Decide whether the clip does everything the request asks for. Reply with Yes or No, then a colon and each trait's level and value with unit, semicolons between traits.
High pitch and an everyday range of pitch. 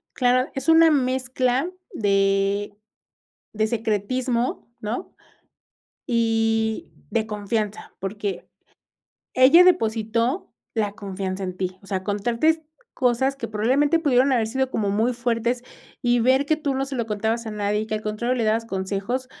Yes: high, 230 Hz; average, 3.6 semitones